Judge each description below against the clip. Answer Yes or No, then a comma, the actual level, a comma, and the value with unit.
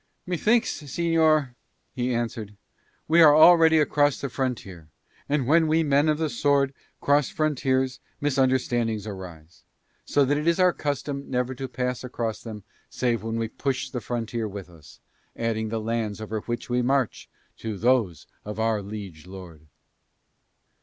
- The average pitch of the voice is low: Yes, low, 125 Hz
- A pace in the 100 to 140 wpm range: No, average, 155 wpm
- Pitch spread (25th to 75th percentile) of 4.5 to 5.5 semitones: Yes, average, 4.9 semitones